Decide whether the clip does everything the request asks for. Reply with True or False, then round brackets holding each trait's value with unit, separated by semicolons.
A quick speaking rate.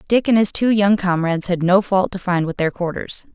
True (250 wpm)